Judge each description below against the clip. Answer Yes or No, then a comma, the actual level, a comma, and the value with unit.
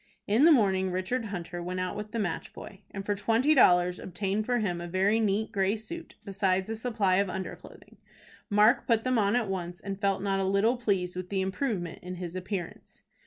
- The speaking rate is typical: No, fast, 215 wpm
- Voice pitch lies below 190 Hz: No, high, 195 Hz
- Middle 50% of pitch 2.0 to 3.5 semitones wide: Yes, average, 3.1 semitones